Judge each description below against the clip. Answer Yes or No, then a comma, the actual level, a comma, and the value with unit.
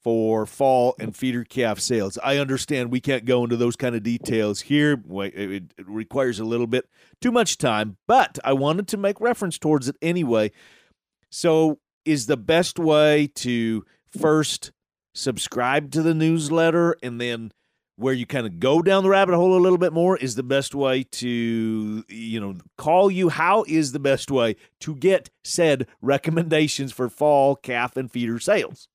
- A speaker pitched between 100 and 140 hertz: Yes, low, 135 Hz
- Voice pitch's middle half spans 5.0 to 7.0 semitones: Yes, average, 5.3 semitones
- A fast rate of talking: No, average, 175 wpm